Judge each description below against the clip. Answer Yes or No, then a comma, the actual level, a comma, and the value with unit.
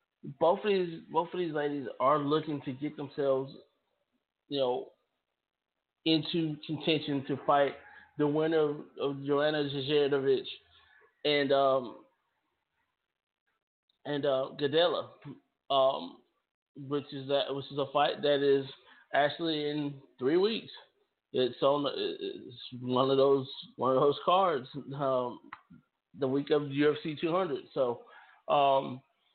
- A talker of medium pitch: Yes, medium, 145 Hz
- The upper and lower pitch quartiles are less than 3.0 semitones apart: Yes, narrow, 2.5 semitones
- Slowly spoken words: Yes, slow, 125 wpm